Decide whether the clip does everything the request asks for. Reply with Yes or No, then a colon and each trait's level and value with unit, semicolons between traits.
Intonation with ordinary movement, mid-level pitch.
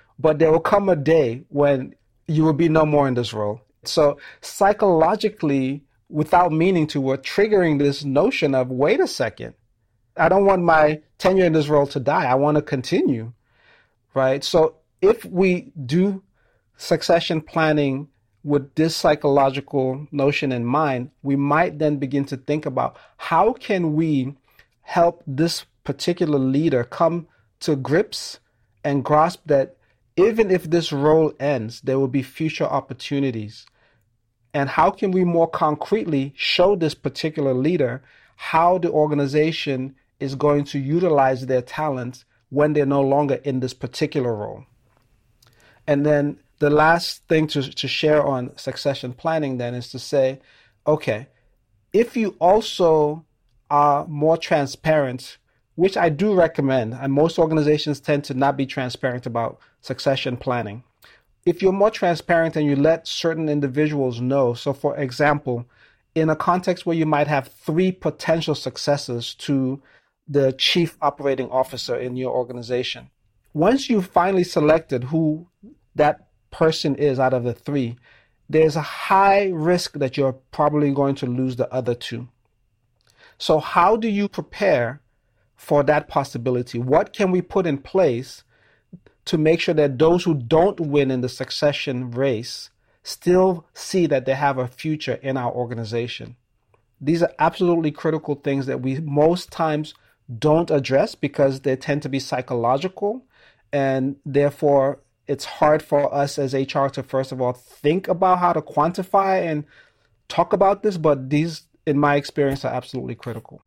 Yes: average, 3.6 semitones; medium, 145 Hz